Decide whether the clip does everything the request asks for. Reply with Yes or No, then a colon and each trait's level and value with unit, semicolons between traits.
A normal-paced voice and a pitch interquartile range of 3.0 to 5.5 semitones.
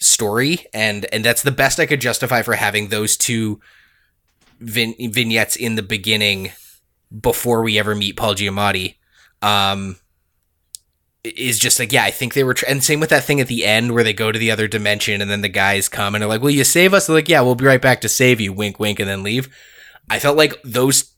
No: fast, 225 wpm; average, 3.7 semitones